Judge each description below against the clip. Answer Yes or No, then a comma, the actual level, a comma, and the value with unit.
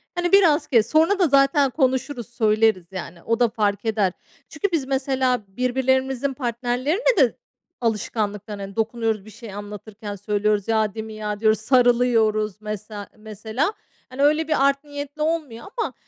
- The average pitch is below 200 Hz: No, high, 235 Hz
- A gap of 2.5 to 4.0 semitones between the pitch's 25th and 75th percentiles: No, average, 4.4 semitones